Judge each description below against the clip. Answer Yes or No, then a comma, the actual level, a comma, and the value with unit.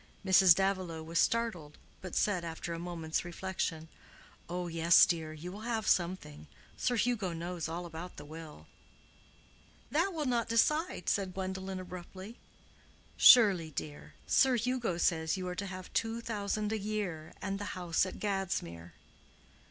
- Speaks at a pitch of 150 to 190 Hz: Yes, medium, 185 Hz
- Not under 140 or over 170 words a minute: Yes, average, 150 wpm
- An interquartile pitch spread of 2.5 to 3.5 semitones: No, average, 4.0 semitones